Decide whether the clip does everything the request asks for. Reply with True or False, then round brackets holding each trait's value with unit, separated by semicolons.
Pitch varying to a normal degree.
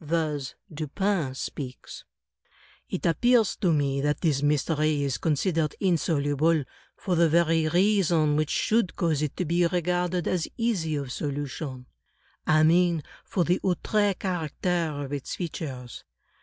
True (3.5 semitones)